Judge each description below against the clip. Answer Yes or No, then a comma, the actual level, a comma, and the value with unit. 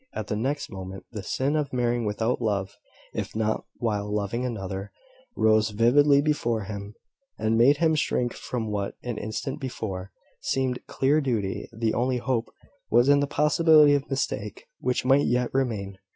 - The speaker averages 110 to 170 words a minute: Yes, average, 165 wpm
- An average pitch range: Yes, average, 4.2 semitones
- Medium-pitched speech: No, low, 120 Hz